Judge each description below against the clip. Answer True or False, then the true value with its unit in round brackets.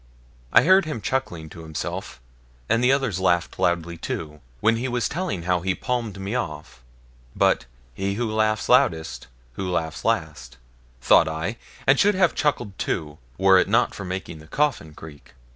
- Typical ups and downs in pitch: False (7.2 semitones)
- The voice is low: True (95 Hz)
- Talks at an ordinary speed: True (165 wpm)